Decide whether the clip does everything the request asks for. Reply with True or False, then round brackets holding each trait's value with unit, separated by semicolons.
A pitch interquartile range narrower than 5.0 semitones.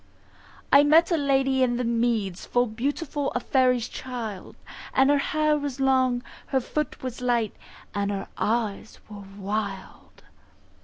True (3.8 semitones)